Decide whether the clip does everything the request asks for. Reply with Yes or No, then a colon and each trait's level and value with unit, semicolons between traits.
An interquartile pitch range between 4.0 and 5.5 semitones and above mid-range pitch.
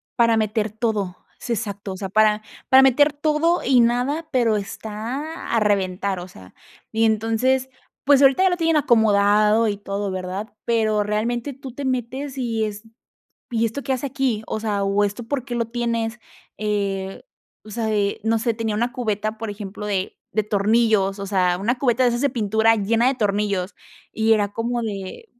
No: average, 3.0 semitones; high, 220 Hz